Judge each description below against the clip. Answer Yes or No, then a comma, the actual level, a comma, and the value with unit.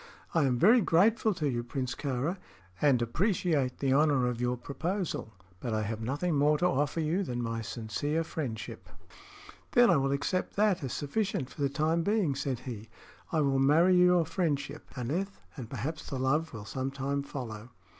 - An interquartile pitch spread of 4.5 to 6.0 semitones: Yes, average, 5.0 semitones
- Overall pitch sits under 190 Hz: Yes, medium, 140 Hz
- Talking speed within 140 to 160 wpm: No, average, 180 wpm